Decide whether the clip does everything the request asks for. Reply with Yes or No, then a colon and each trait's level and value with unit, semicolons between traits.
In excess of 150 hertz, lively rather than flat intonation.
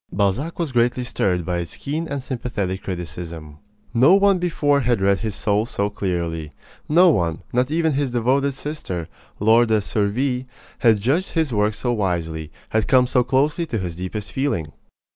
No: low, 115 Hz; wide, 6.7 semitones